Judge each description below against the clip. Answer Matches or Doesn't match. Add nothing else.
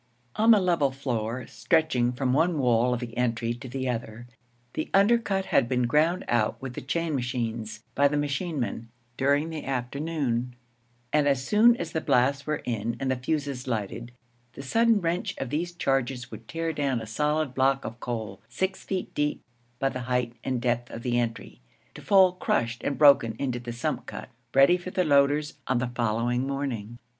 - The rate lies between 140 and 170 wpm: Doesn't match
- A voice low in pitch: Matches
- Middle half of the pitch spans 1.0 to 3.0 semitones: Doesn't match